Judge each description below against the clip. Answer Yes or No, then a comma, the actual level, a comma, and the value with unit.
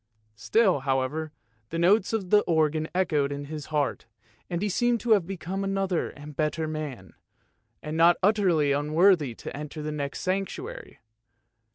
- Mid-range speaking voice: Yes, medium, 160 Hz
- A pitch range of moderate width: Yes, average, 4.8 semitones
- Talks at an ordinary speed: Yes, average, 160 wpm